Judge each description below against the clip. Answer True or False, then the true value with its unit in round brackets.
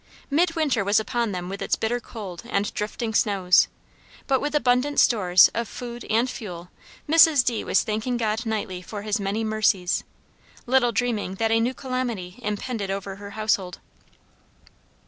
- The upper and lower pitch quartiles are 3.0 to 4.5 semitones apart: True (3.7 semitones)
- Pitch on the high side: True (220 Hz)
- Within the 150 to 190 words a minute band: True (155 wpm)